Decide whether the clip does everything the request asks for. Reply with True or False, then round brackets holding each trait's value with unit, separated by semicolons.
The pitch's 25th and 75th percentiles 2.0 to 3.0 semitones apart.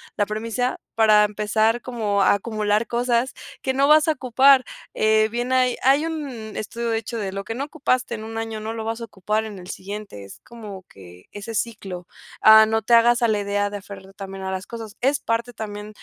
True (2.6 semitones)